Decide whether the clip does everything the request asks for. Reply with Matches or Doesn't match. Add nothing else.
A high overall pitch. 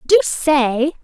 Matches